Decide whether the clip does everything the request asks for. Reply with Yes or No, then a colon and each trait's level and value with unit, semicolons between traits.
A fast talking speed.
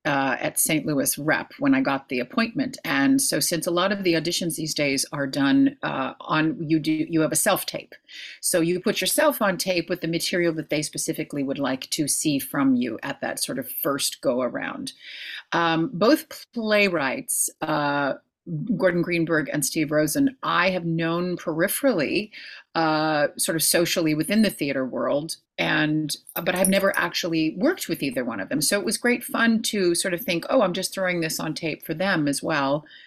No: average, 195 wpm